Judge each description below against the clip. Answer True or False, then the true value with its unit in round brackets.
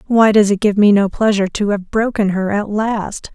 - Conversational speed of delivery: False (235 wpm)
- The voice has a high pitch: True (205 Hz)